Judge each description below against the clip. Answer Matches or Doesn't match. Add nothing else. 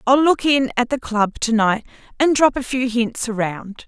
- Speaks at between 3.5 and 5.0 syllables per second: Matches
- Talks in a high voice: Matches